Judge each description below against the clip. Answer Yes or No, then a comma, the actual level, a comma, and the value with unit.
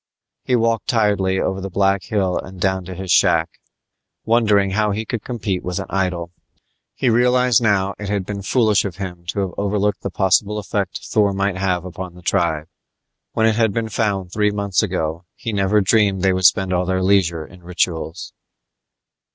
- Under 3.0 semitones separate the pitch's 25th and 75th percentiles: Yes, narrow, 2.4 semitones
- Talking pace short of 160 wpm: No, average, 185 wpm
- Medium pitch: No, very low, 95 Hz